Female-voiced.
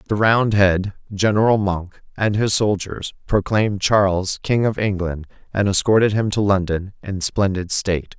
No: male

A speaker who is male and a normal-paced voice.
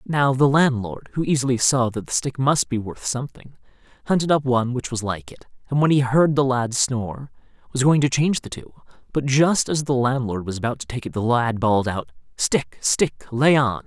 No: male; fast, 220 wpm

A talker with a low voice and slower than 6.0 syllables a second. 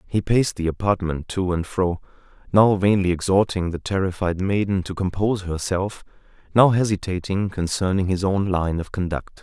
Yes: very low, 95 Hz; 5.1 syllables/s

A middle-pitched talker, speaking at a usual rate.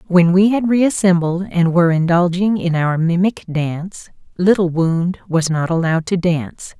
Yes: medium, 175 Hz; average, 160 wpm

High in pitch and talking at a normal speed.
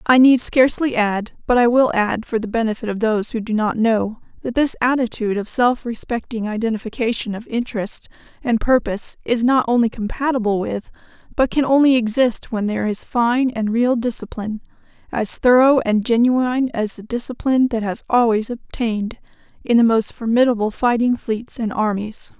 Yes: high, 230 Hz; average, 170 wpm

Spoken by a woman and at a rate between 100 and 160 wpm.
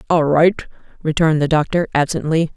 Yes: female; average, 140 wpm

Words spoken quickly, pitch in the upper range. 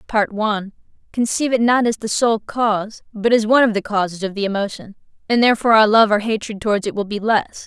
Yes: fast, 225 wpm; high, 215 Hz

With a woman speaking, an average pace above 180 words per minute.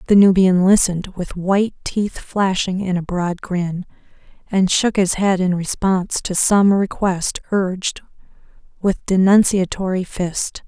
No: female; slow, 135 wpm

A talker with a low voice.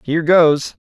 No: medium, 160 Hz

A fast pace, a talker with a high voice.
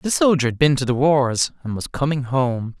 No: fast, 235 wpm; low, 135 Hz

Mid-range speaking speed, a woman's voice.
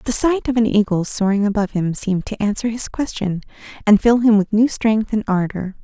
No: fast, 215 wpm; female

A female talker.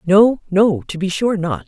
Yes: female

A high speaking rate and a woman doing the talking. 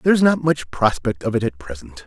No: fast, 260 wpm; male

